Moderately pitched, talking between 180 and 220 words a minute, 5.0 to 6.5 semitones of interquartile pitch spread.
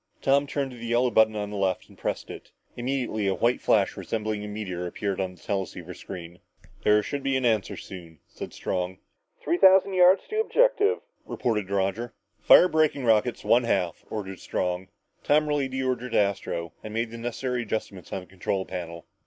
No: low, 110 Hz; average, 190 wpm; wide, 5.6 semitones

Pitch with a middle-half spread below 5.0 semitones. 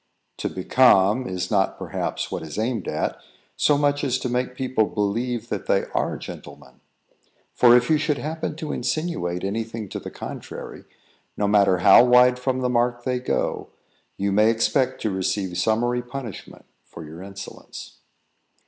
Yes: average, 4.2 semitones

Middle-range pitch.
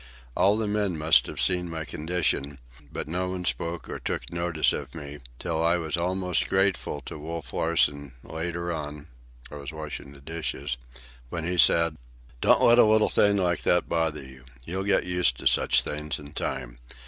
No: very low, 85 Hz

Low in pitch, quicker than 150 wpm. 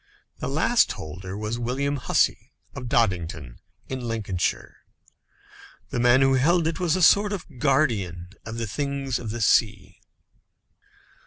No: low, 120 Hz; average, 140 wpm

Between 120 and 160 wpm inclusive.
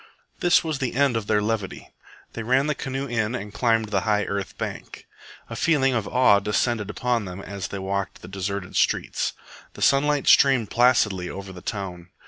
No: average, 185 wpm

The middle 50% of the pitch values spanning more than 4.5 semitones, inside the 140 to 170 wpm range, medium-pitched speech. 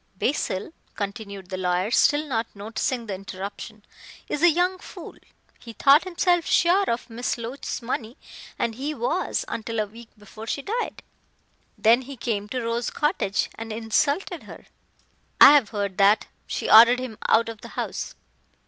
No: average, 5.1 semitones; average, 165 wpm; high, 230 Hz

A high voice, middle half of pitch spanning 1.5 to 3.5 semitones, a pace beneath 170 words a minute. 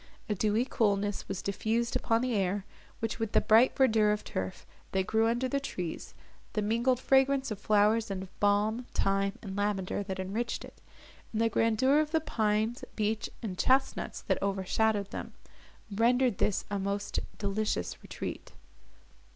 Yes: high, 215 Hz; average, 2.7 semitones; average, 160 wpm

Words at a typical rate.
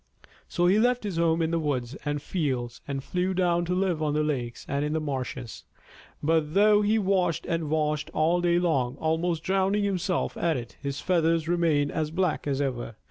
Yes: average, 195 wpm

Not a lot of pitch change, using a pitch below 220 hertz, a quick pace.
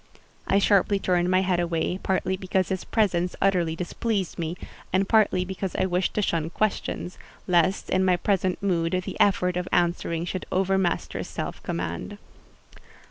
No: narrow, 1.7 semitones; medium, 185 Hz; average, 155 wpm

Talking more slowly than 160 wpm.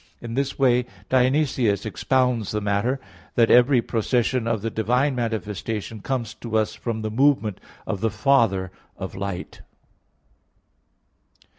Yes: average, 145 wpm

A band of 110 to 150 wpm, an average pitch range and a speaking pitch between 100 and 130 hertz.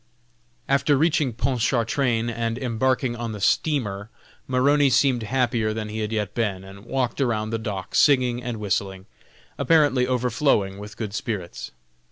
Yes: average, 145 wpm; average, 3.5 semitones; low, 115 Hz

